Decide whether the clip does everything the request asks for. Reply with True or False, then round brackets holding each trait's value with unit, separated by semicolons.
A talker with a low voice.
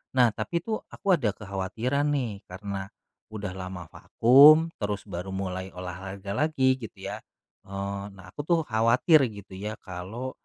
True (105 Hz)